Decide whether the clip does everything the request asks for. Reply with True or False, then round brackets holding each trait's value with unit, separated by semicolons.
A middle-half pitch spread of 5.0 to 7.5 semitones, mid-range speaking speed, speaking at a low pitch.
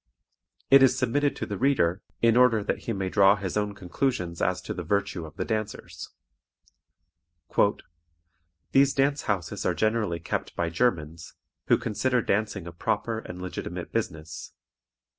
True (5.6 semitones; 150 wpm; 105 Hz)